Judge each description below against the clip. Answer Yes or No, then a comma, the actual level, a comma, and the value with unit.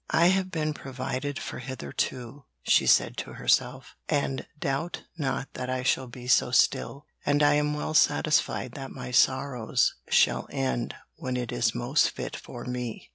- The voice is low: Yes, low, 130 Hz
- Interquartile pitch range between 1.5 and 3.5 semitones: Yes, average, 2.9 semitones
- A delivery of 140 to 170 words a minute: Yes, average, 165 wpm